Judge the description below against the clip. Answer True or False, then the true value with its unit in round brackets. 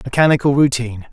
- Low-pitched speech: True (130 Hz)